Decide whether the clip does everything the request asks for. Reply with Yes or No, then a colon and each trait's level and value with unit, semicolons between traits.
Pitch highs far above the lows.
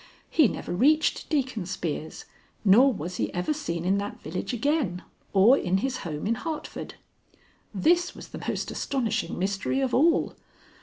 Yes: wide, 7.4 semitones